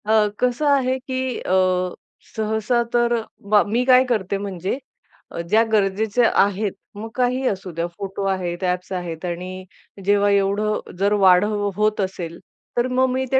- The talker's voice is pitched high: Yes, high, 205 Hz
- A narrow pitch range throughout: No, average, 4.2 semitones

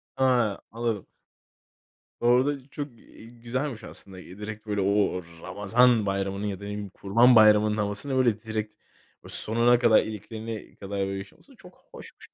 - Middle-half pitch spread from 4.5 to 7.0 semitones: No, average, 2.9 semitones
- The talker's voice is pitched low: Yes, low, 110 Hz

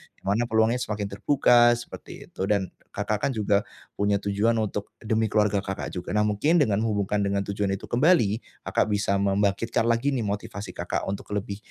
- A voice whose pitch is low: Yes, low, 105 Hz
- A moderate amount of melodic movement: No, narrow, 2.3 semitones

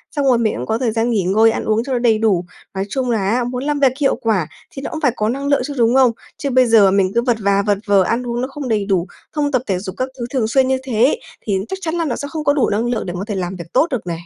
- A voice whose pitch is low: No, high, 235 Hz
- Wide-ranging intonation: No, average, 4.7 semitones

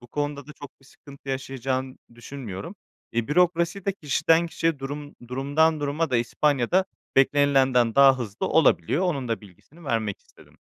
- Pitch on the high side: No, medium, 140 Hz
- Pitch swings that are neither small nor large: Yes, average, 3.4 semitones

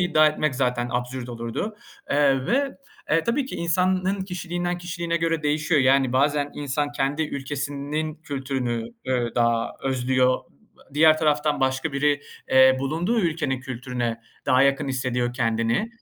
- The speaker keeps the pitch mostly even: No, average, 3.7 semitones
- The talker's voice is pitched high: No, medium, 140 Hz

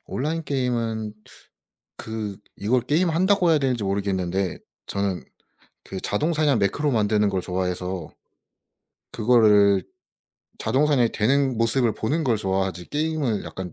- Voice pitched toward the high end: No, low, 110 Hz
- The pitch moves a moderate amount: No, wide, 6.1 semitones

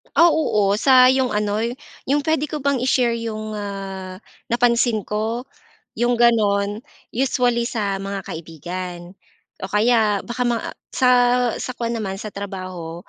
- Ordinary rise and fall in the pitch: Yes, average, 3.6 semitones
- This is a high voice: Yes, high, 220 Hz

